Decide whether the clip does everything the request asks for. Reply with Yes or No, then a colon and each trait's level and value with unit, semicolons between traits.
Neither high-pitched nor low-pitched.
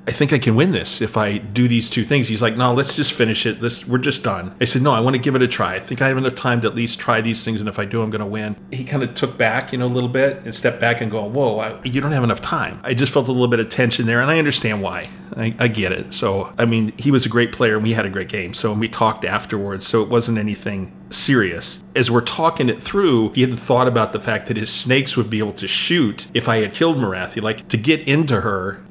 No: low, 115 Hz